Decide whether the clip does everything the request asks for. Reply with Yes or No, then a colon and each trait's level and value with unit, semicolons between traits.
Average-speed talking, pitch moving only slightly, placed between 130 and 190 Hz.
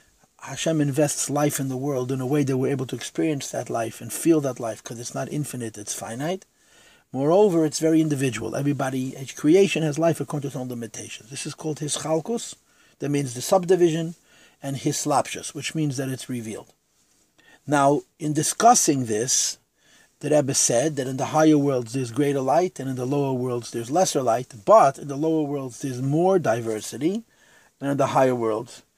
No: average, 195 wpm; average, 3.3 semitones; medium, 140 Hz